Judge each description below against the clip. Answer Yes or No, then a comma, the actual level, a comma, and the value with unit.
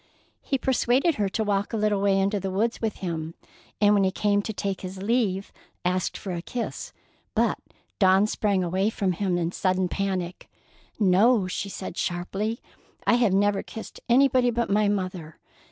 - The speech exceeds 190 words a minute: No, average, 175 wpm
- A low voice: No, high, 200 Hz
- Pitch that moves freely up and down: No, average, 2.8 semitones